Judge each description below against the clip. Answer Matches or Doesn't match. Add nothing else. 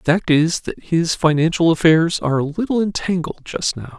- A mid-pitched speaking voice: Matches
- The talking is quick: Doesn't match